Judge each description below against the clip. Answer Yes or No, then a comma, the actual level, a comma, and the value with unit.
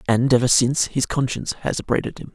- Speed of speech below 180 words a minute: No, fast, 205 wpm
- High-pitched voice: No, low, 130 Hz